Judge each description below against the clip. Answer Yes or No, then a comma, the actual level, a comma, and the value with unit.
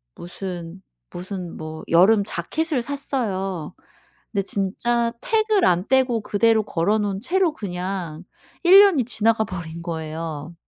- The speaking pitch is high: Yes, high, 195 Hz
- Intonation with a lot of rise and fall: Yes, wide, 5.7 semitones